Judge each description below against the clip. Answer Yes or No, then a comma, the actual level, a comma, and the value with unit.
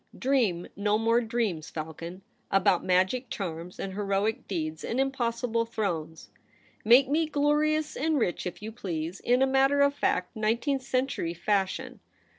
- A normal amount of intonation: No, wide, 6.5 semitones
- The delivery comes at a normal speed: Yes, average, 150 wpm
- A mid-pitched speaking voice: No, high, 220 Hz